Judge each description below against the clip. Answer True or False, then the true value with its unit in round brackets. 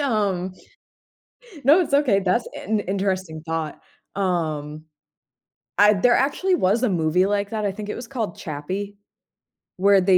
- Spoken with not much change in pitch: False (3.3 semitones)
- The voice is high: True (200 Hz)